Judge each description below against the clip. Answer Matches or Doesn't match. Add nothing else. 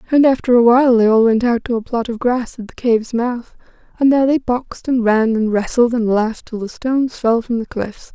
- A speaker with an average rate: Doesn't match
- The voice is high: Matches